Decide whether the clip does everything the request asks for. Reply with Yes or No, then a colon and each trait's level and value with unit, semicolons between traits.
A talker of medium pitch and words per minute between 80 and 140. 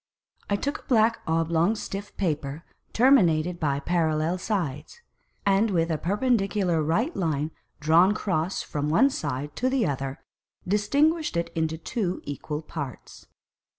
Yes: medium, 170 Hz; slow, 135 wpm